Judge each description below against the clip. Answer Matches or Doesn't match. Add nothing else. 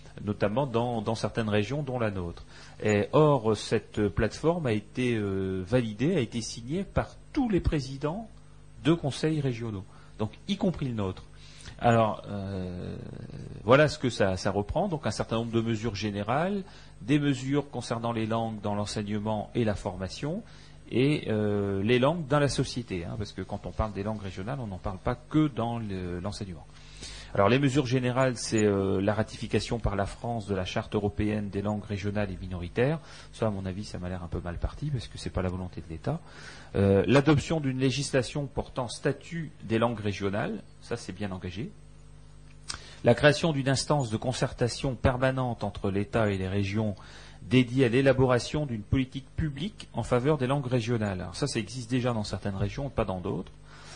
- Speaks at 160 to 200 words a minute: Matches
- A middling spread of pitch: Matches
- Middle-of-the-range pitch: Doesn't match